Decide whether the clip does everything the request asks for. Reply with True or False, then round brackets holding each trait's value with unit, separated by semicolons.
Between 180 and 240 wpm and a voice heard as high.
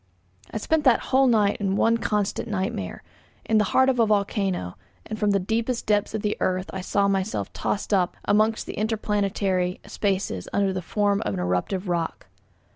True (185 wpm; 205 Hz)